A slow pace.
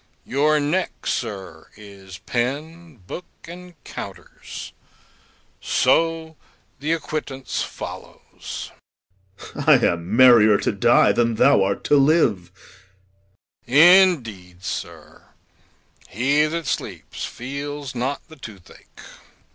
Yes: slow, 100 wpm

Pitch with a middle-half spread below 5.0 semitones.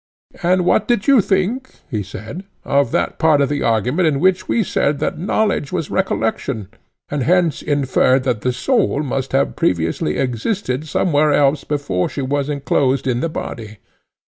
No: wide, 5.5 semitones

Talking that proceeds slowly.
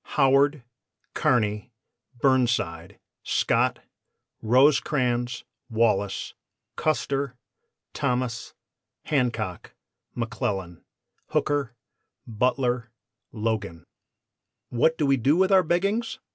Yes: slow, 75 wpm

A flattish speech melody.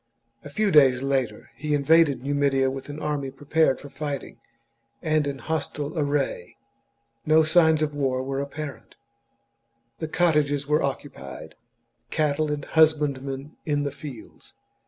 Yes: narrow, 2.1 semitones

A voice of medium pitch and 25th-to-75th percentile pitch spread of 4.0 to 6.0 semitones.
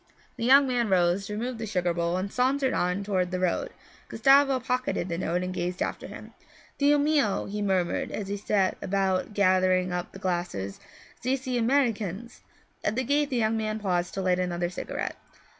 No: high, 200 Hz; wide, 5.4 semitones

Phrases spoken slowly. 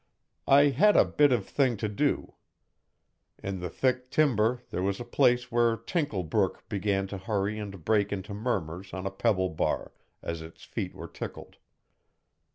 No: average, 170 wpm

